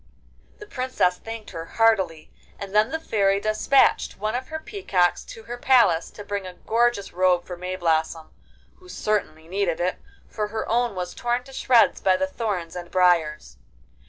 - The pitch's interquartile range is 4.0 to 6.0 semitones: Yes, average, 5.1 semitones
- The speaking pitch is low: No, high, 200 Hz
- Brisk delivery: No, average, 170 wpm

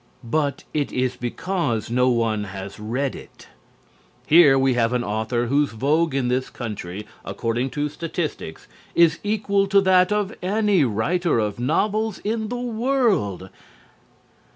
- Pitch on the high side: No, medium, 140 Hz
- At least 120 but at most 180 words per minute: Yes, average, 140 wpm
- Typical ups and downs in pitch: No, wide, 8.3 semitones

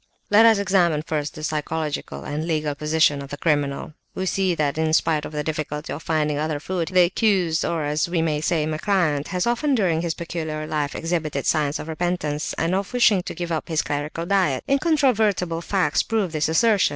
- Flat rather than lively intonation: No, average, 3.4 semitones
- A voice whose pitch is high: No, medium, 160 Hz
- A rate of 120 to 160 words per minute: No, average, 200 wpm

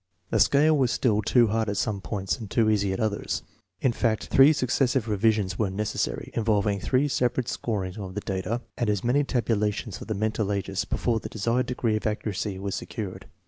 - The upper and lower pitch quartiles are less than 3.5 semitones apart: Yes, average, 3.1 semitones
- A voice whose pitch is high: No, low, 110 Hz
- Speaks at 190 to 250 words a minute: Yes, average, 200 wpm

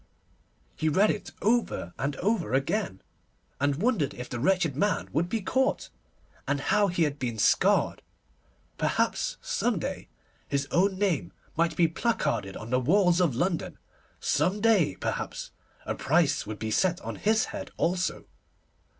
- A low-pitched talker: No, medium, 170 Hz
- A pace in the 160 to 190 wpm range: No, average, 150 wpm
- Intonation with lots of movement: Yes, wide, 6.4 semitones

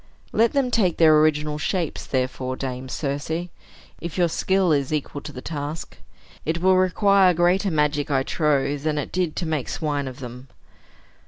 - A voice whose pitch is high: No, medium, 155 Hz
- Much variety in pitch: No, average, 3.9 semitones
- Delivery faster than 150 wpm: Yes, average, 170 wpm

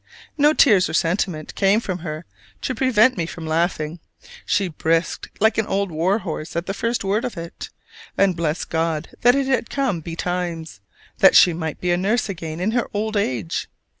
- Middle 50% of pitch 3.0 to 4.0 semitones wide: No, average, 4.6 semitones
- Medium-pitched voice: Yes, medium, 180 Hz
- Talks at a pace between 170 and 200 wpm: Yes, average, 185 wpm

